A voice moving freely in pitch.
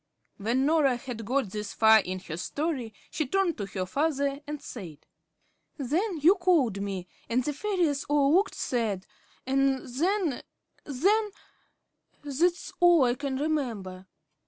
Yes: wide, 6.2 semitones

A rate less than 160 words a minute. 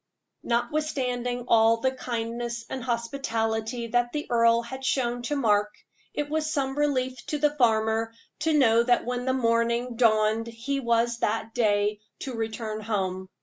Yes: average, 150 wpm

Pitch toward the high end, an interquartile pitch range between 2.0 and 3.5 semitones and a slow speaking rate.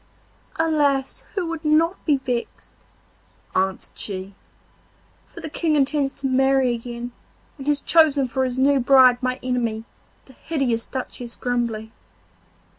Yes: very high, 265 Hz; average, 3.2 semitones; slow, 130 wpm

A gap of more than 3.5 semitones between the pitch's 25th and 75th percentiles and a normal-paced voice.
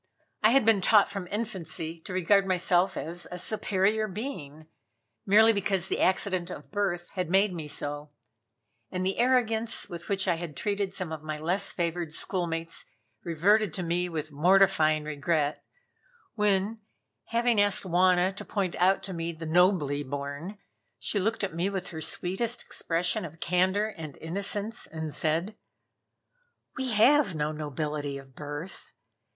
Yes: average, 4.0 semitones; average, 155 wpm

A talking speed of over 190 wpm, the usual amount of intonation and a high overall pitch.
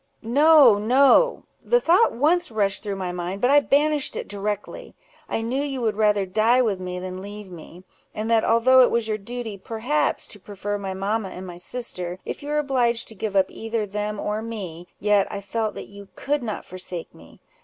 Yes: average, 200 wpm; average, 4.1 semitones; high, 215 Hz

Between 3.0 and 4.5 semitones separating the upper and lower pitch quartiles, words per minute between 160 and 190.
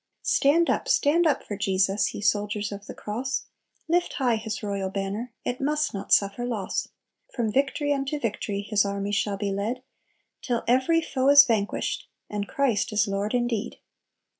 No: average, 4.9 semitones; average, 165 wpm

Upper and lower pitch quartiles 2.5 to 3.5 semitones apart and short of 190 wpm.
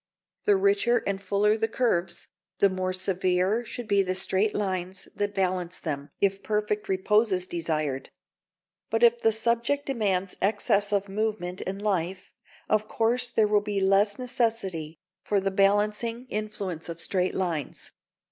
Yes: average, 2.9 semitones; average, 150 wpm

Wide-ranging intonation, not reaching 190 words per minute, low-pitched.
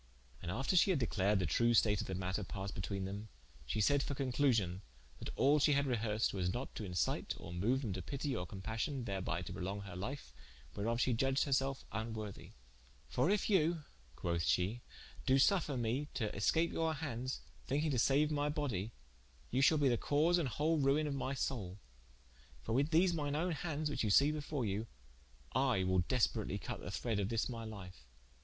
No: wide, 6.4 semitones; average, 200 wpm; low, 120 Hz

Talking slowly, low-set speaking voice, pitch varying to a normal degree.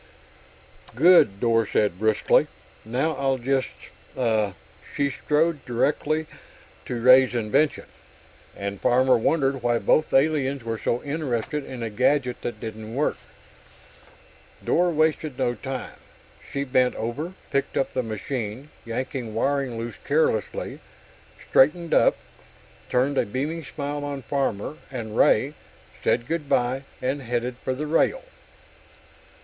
Yes: slow, 125 wpm; low, 130 Hz; average, 3.7 semitones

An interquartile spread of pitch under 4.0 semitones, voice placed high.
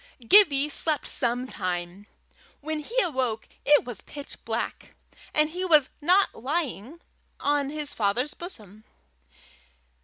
No: average, 4.9 semitones; very high, 285 Hz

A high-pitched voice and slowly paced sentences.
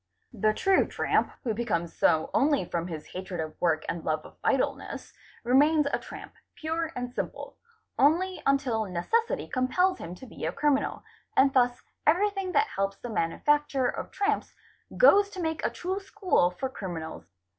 No: very high, 260 Hz; average, 165 wpm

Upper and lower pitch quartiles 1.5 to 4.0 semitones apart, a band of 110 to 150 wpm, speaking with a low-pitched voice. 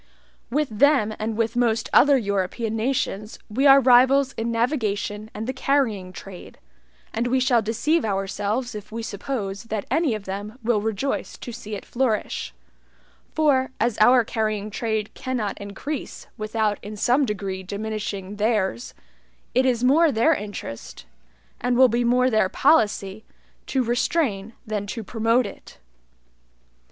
No: average, 3.5 semitones; average, 145 wpm; high, 225 Hz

